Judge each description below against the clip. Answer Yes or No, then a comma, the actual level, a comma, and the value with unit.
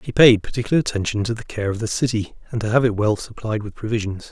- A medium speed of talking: No, fast, 250 wpm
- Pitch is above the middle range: No, low, 110 Hz